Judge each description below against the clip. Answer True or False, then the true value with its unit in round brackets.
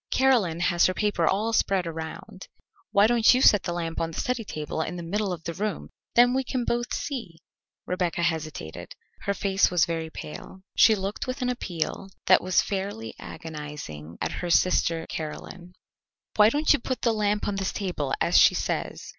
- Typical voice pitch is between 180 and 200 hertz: True (185 Hz)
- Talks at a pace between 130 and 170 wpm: False (190 wpm)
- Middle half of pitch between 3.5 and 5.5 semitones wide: True (4.6 semitones)